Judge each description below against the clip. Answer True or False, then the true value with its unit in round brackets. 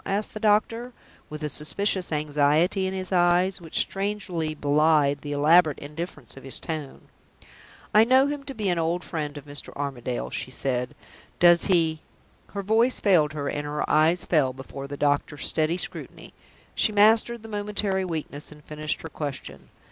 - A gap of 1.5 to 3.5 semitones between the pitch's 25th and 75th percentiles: False (4.9 semitones)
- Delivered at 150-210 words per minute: True (170 wpm)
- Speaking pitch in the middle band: True (160 Hz)